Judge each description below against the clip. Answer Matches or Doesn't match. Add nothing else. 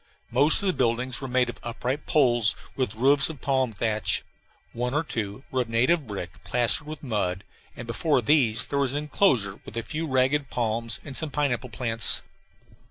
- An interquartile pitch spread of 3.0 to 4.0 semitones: Matches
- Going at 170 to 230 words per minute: Matches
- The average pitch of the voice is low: Matches